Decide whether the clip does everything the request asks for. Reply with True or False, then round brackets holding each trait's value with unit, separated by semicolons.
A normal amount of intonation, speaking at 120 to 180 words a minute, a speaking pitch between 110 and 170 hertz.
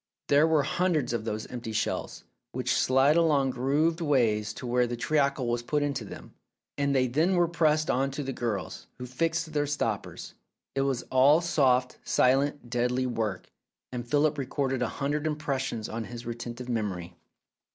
True (3.7 semitones; 170 wpm; 135 Hz)